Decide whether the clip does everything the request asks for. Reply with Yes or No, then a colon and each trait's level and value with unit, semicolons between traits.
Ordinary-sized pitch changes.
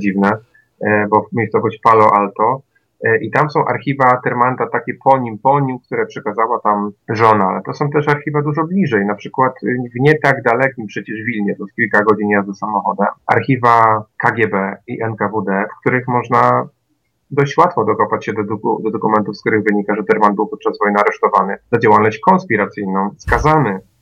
Yes: average, 3.8 semitones